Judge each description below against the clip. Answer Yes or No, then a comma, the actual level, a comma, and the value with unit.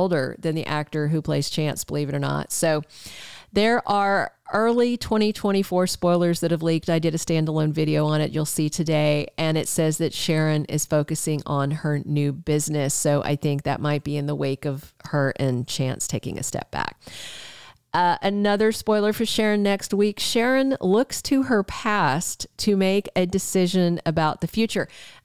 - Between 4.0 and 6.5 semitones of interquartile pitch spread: Yes, average, 4.8 semitones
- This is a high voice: No, medium, 160 Hz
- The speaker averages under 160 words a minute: No, average, 185 wpm